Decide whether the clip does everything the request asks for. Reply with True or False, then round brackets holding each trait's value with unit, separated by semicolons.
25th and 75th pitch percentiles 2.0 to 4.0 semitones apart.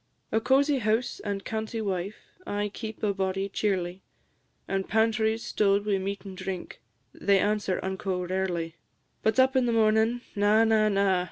True (2.4 semitones)